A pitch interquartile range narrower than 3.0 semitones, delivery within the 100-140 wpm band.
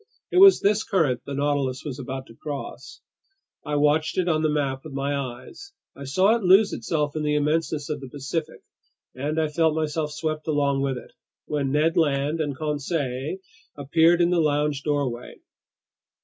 No: narrow, 2.4 semitones; average, 175 wpm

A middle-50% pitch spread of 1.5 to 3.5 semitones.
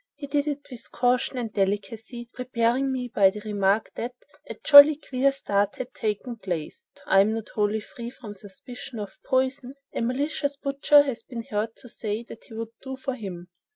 No: average, 4.1 semitones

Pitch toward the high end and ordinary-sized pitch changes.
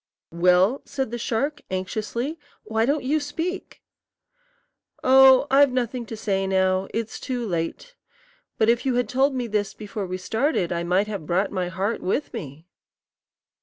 No: high, 225 Hz; wide, 5.8 semitones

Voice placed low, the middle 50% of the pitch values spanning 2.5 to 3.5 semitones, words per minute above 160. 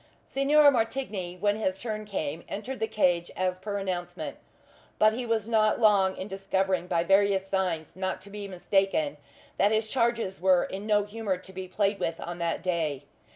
No: high, 195 Hz; average, 2.8 semitones; average, 180 wpm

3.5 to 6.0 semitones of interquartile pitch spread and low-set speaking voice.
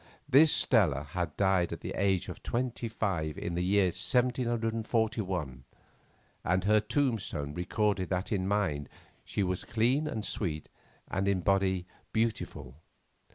Yes: average, 4.2 semitones; low, 100 Hz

